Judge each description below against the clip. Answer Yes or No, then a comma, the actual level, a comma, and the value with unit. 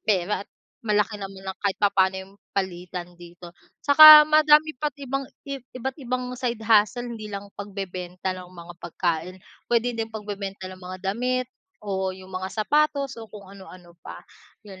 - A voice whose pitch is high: Yes, high, 200 Hz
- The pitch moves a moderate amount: Yes, average, 4.7 semitones